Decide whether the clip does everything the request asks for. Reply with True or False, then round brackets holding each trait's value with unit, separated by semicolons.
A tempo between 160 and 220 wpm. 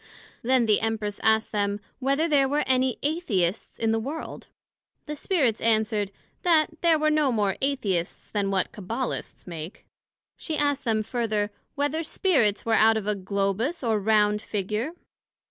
False (150 wpm)